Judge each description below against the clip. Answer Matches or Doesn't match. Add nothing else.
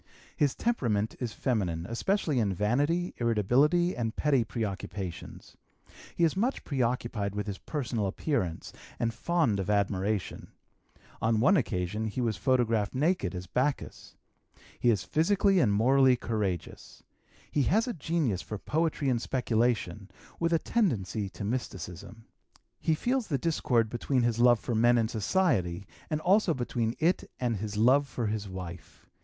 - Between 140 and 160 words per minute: Matches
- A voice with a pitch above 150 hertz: Doesn't match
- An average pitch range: Doesn't match